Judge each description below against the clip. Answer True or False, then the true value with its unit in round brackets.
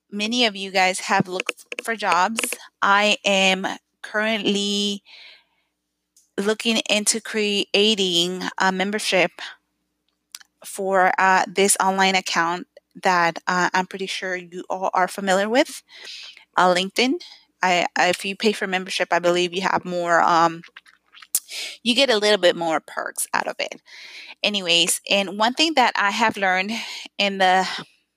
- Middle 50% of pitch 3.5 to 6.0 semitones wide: False (3.0 semitones)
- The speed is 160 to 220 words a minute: False (140 wpm)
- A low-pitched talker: False (195 Hz)